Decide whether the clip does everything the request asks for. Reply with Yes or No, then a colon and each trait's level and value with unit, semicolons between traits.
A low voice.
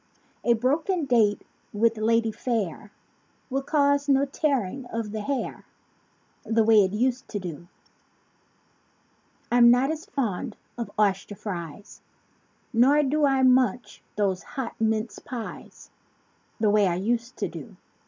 No: high, 230 Hz